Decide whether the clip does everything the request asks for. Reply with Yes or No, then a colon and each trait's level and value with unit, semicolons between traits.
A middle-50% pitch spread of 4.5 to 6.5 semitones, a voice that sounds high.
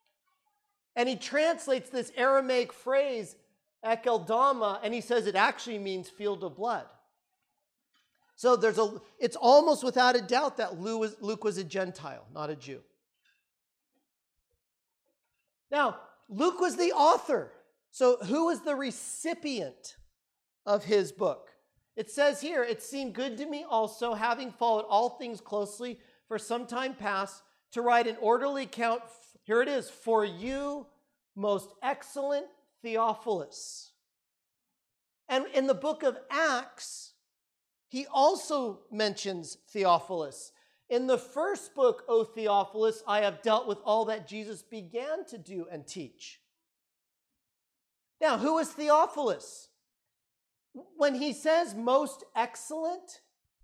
Yes: average, 4.9 semitones; high, 245 Hz